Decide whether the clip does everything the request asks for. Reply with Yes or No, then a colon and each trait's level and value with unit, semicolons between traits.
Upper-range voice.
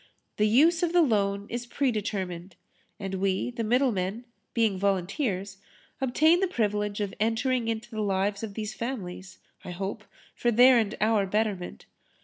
Yes: high, 215 Hz